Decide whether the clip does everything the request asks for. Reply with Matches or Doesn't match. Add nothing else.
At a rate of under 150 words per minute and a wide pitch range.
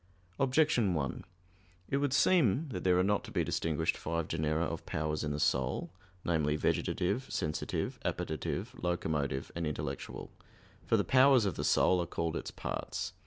Doesn't match